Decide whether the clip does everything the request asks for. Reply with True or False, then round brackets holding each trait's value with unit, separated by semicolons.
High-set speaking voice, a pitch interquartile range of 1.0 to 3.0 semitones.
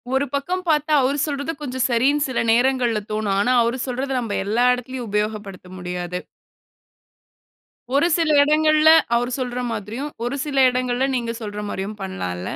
False (245 Hz; 4.8 semitones)